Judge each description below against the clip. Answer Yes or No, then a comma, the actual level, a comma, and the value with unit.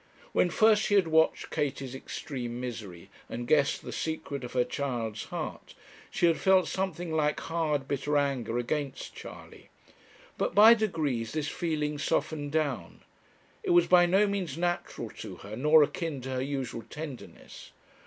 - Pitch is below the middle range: No, medium, 150 Hz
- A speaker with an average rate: Yes, average, 155 wpm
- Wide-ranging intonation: No, average, 4.7 semitones